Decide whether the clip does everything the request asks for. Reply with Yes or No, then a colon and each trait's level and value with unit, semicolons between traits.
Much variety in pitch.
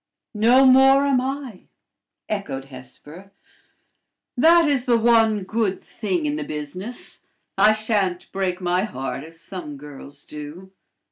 Yes: wide, 7.8 semitones